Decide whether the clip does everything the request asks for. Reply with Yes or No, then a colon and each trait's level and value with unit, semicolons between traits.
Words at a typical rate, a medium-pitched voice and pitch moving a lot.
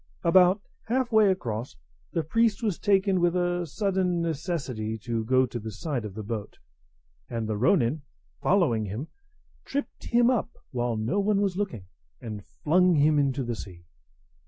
Yes: average, 160 wpm; medium, 160 Hz; wide, 8.7 semitones